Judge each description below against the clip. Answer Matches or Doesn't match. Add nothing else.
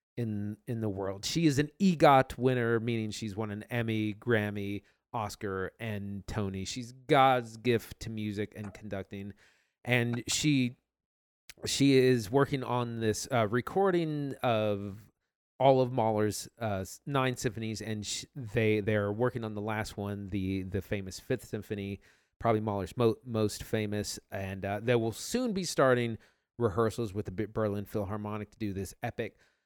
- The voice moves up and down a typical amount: Matches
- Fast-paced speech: Doesn't match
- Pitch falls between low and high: Doesn't match